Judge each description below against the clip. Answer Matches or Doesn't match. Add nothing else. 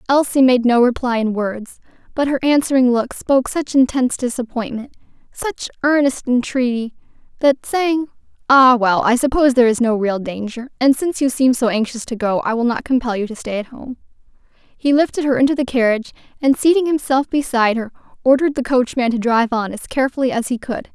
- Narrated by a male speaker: Doesn't match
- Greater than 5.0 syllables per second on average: Matches